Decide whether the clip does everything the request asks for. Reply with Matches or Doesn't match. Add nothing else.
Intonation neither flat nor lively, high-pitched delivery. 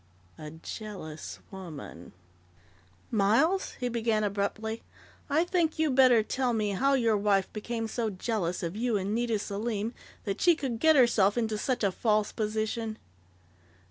Matches